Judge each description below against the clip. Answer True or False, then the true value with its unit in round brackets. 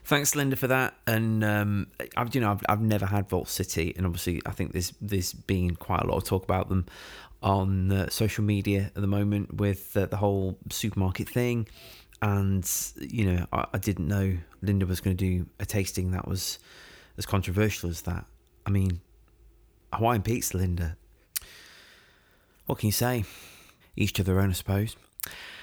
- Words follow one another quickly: False (180 wpm)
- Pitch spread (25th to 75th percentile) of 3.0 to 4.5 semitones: False (2.4 semitones)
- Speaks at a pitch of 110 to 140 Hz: False (100 Hz)